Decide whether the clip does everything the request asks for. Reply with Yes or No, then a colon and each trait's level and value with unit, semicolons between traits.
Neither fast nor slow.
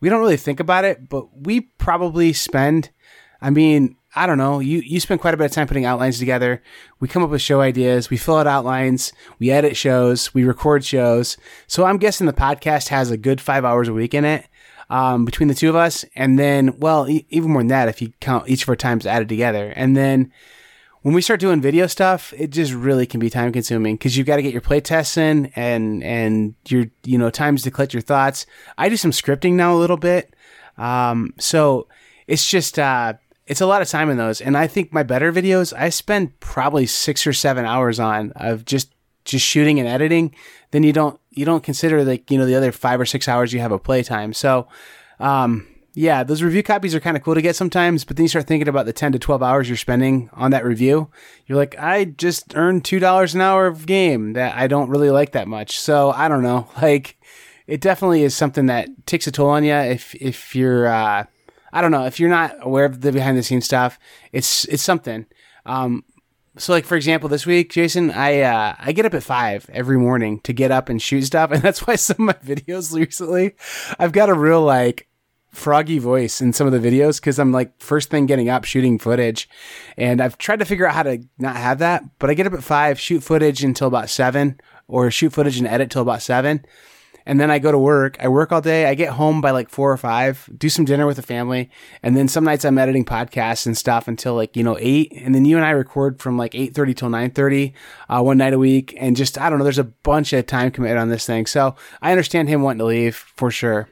No: fast, 240 wpm